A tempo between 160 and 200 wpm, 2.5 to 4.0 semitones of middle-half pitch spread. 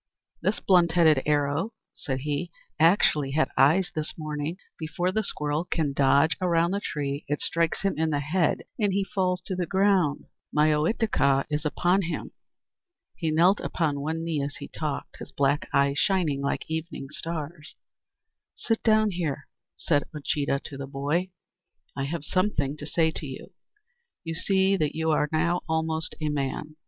Yes: average, 170 wpm; average, 3.4 semitones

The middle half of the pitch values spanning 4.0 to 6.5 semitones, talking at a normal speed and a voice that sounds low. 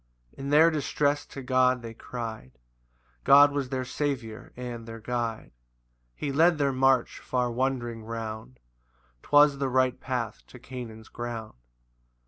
No: average, 3.1 semitones; average, 145 wpm; low, 125 Hz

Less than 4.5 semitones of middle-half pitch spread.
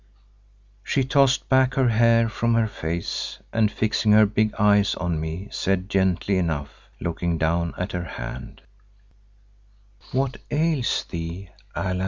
No: average, 5.2 semitones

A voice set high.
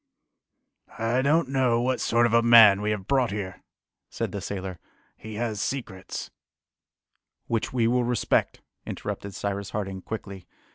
No: low, 110 Hz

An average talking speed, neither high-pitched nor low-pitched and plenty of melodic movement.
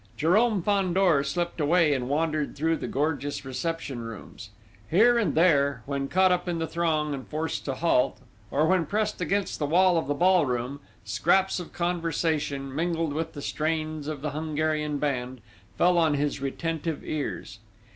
No: average, 165 wpm; medium, 155 Hz; average, 3.3 semitones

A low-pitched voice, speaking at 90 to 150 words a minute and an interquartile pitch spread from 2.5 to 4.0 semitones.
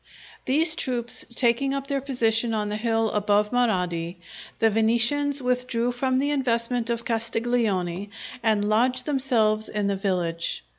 No: high, 230 Hz; average, 140 wpm; average, 3.2 semitones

